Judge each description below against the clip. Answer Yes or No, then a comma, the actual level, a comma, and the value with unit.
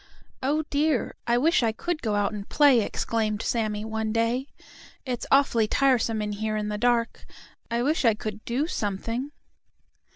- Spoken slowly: No, average, 165 wpm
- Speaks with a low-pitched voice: No, high, 230 Hz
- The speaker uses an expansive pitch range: No, average, 3.8 semitones